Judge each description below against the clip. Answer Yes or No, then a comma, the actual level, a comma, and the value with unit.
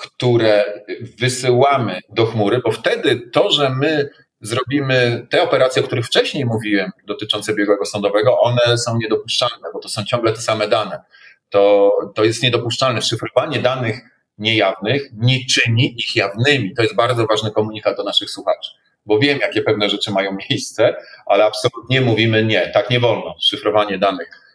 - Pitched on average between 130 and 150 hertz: No, low, 110 Hz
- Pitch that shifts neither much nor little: Yes, average, 3.4 semitones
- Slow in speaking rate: No, average, 155 wpm